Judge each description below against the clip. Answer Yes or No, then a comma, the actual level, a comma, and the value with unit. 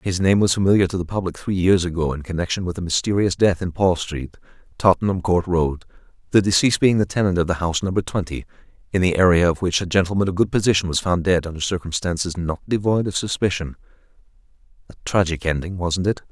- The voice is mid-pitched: No, very low, 90 Hz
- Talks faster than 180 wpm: Yes, fast, 205 wpm